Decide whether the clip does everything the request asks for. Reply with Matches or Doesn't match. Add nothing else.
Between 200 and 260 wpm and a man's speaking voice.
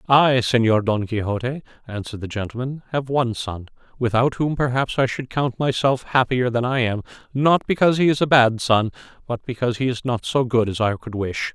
Matches